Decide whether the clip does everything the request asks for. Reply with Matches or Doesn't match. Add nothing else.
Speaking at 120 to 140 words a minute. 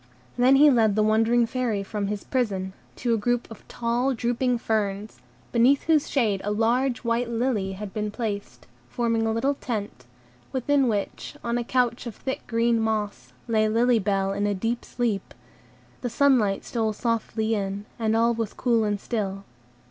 Doesn't match